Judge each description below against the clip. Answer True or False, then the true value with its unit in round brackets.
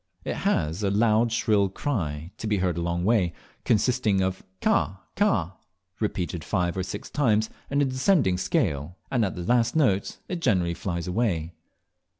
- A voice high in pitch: False (100 Hz)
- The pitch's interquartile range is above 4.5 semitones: True (5.1 semitones)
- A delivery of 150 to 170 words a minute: True (165 wpm)